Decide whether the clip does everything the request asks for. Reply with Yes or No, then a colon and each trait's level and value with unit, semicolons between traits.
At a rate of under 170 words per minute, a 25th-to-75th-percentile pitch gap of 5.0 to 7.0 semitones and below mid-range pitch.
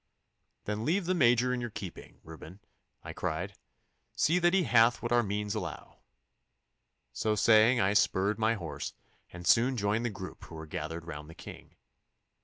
No: average, 175 wpm; wide, 5.4 semitones; low, 110 Hz